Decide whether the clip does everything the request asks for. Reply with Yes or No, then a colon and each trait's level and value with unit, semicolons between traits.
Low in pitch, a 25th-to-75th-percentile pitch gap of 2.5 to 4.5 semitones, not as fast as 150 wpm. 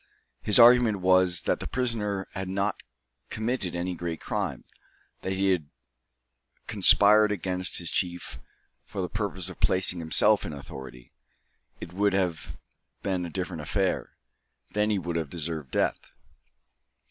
Yes: very low, 95 Hz; average, 3.1 semitones; average, 140 wpm